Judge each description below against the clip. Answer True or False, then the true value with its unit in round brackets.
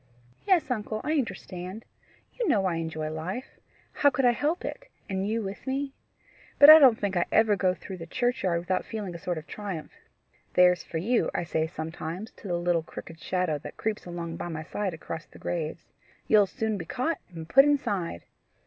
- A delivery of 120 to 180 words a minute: False (195 wpm)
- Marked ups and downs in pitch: True (6.0 semitones)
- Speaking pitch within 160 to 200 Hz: True (190 Hz)